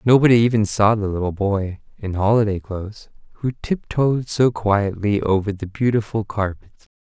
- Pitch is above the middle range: No, low, 105 Hz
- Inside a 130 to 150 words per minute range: Yes, average, 145 wpm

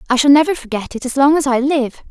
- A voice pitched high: Yes, very high, 270 Hz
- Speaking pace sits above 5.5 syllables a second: Yes, 6.5 syllables/s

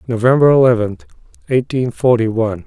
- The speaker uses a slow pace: Yes, slow, 110 wpm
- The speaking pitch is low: Yes, low, 120 Hz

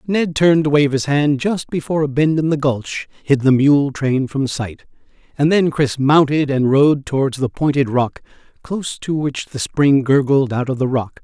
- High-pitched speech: No, medium, 140 Hz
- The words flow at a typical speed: No, fast, 210 wpm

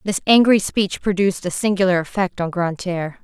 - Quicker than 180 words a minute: No, average, 165 wpm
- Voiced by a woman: Yes, female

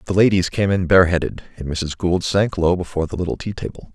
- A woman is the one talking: No, male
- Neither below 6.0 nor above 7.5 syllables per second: Yes, 6.3 syllables/s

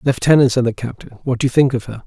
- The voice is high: No, low, 125 Hz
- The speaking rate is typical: No, fast, 290 wpm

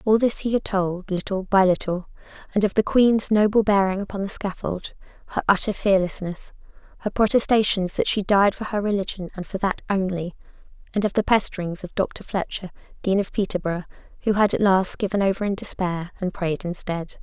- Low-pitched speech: No, high, 195 Hz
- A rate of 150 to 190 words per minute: Yes, average, 185 wpm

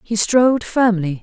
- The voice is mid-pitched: No, high, 220 Hz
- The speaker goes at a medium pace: Yes, average, 145 wpm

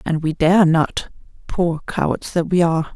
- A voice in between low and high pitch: Yes, medium, 170 Hz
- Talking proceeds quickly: No, average, 185 wpm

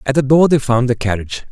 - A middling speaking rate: No, fast, 275 wpm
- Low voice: Yes, low, 130 Hz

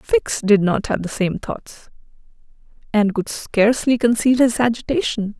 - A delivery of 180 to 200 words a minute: No, average, 145 wpm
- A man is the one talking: No, female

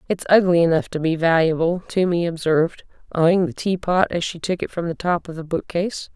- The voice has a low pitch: No, medium, 170 Hz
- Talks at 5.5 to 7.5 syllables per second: Yes, 5.6 syllables/s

